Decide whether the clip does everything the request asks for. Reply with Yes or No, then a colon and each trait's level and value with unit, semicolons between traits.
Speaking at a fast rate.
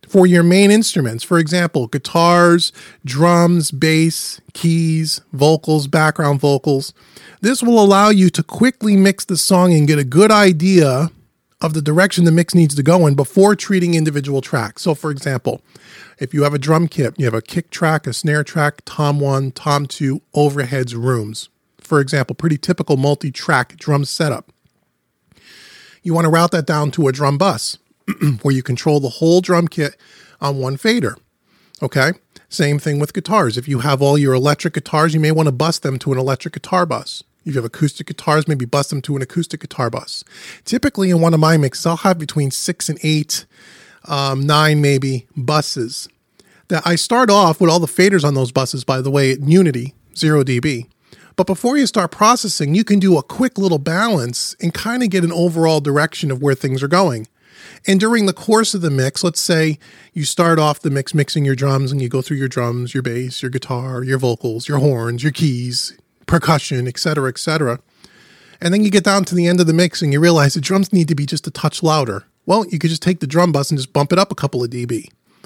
Yes: fast, 210 wpm